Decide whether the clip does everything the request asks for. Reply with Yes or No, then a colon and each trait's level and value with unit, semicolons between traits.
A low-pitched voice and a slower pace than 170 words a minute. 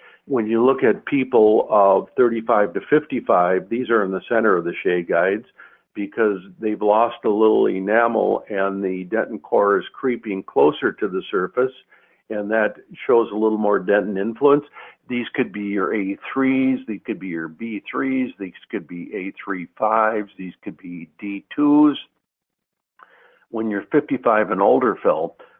Yes: low, 110 Hz; average, 155 wpm